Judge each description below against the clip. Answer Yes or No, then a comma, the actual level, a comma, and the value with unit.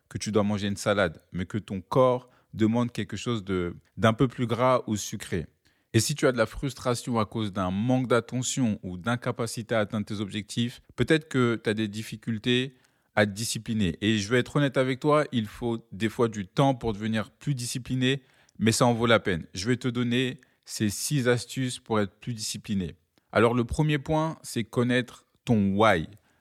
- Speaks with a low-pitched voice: Yes, low, 115 Hz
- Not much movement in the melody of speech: No, average, 3.0 semitones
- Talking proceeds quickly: No, average, 200 wpm